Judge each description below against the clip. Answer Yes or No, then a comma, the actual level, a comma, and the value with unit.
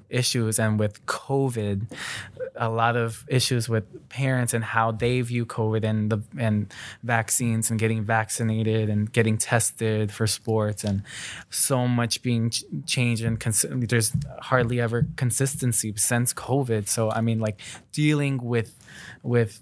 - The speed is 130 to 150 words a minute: Yes, average, 145 wpm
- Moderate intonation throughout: No, narrow, 2.0 semitones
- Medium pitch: No, low, 115 Hz